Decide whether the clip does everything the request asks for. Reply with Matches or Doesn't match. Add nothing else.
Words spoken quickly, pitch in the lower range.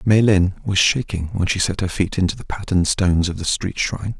Matches